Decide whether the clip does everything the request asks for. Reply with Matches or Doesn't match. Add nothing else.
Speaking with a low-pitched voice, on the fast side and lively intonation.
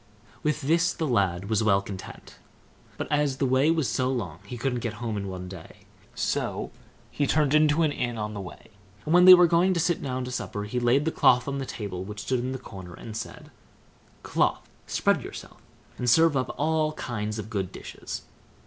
Matches